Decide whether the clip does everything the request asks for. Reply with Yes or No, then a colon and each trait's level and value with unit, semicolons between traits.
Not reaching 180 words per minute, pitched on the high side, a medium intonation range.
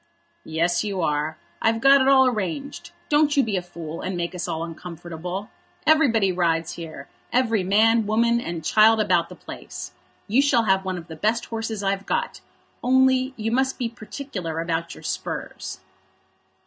No: average, 170 wpm; high, 205 Hz; wide, 5.7 semitones